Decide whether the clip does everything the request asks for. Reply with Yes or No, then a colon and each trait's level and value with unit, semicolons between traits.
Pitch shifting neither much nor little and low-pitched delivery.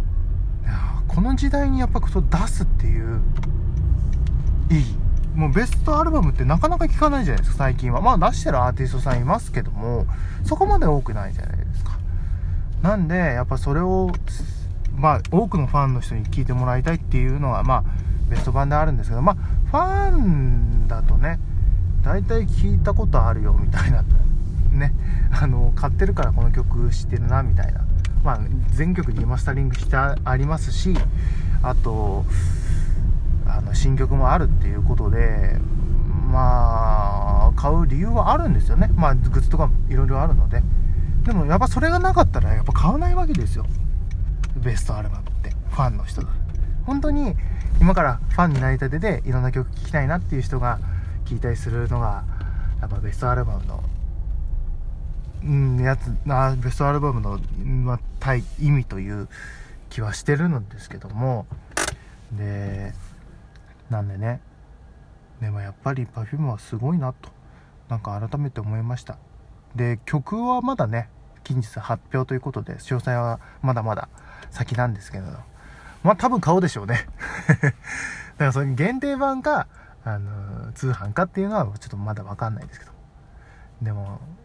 No: wide, 6.5 semitones; low, 110 Hz